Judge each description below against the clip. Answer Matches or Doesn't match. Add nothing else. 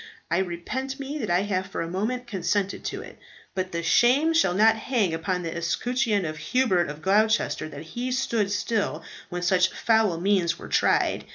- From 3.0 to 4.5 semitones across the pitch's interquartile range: Doesn't match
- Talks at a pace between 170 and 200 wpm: Matches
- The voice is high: Matches